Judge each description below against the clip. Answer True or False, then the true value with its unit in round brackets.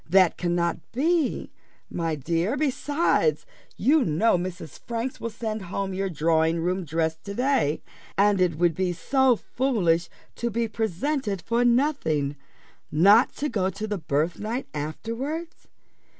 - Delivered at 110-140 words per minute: True (135 wpm)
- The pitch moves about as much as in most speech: False (6.4 semitones)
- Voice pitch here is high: True (195 Hz)